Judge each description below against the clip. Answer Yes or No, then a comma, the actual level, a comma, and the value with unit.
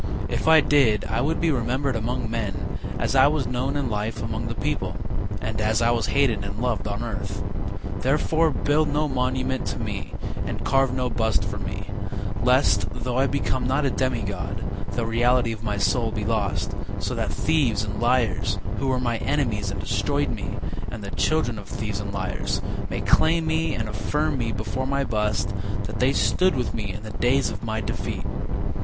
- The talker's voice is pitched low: Yes, low, 120 Hz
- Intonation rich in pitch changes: No, average, 3.9 semitones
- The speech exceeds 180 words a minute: Yes, average, 190 wpm